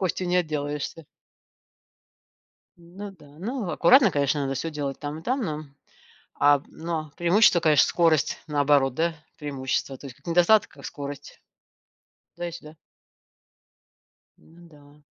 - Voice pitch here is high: No, medium, 155 Hz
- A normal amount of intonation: Yes, average, 3.1 semitones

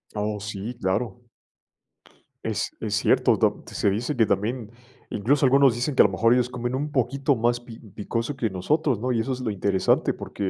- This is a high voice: No, low, 120 Hz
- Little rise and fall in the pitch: No, average, 3.5 semitones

